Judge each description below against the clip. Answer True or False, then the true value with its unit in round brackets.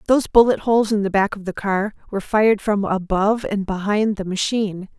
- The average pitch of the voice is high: True (205 Hz)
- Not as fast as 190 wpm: False (205 wpm)